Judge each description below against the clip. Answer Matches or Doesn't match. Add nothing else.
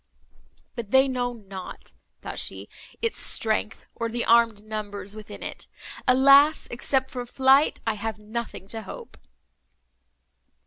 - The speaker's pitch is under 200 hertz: Doesn't match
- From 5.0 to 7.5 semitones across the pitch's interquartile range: Doesn't match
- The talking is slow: Matches